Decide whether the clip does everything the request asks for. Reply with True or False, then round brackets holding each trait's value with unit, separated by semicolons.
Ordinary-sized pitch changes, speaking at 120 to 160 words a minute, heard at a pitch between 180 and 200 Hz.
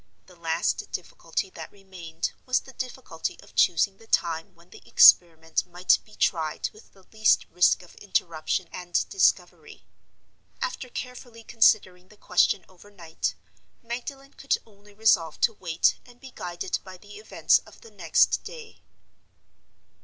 True (4.7 semitones; 145 wpm; 190 Hz)